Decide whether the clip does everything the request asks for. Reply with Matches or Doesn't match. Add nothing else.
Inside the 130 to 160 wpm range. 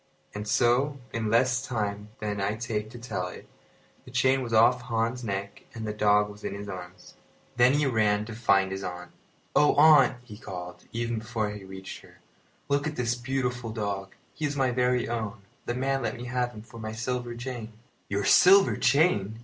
Doesn't match